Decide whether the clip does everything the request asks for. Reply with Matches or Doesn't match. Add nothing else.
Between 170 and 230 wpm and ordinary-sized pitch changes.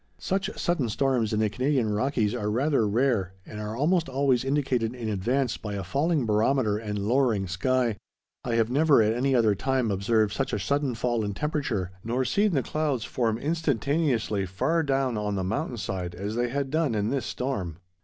Matches